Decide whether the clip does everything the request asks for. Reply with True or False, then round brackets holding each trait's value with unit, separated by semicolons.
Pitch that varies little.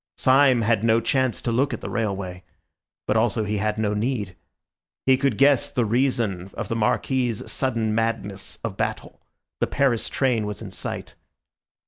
False (3.6 semitones)